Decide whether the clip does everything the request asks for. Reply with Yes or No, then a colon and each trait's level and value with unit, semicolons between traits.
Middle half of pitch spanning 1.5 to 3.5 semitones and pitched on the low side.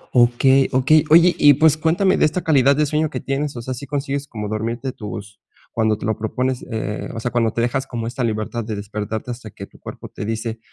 No: average, 4.2 semitones; low, 125 Hz